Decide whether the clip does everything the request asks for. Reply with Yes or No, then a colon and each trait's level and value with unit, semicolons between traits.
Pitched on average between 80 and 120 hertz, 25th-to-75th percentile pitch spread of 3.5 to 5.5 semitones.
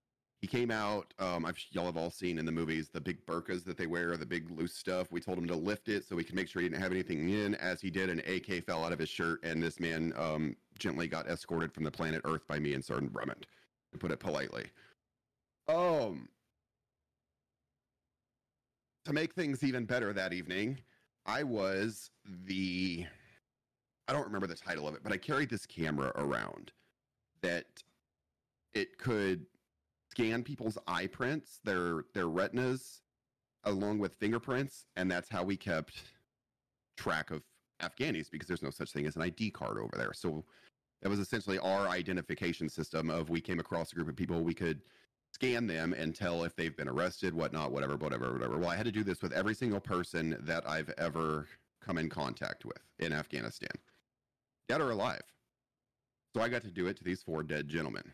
Yes: very low, 90 Hz; average, 4.1 semitones